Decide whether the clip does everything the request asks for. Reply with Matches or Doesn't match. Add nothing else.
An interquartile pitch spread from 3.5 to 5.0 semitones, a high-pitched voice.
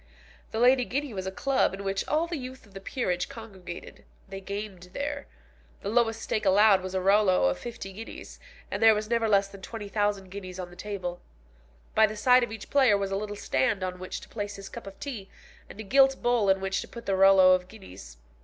Doesn't match